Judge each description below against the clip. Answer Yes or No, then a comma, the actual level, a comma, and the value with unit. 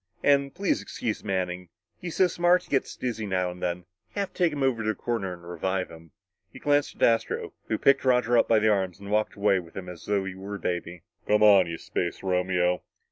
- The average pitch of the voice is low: Yes, low, 100 Hz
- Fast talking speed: Yes, fast, 245 wpm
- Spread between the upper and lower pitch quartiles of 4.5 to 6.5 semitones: Yes, wide, 5.4 semitones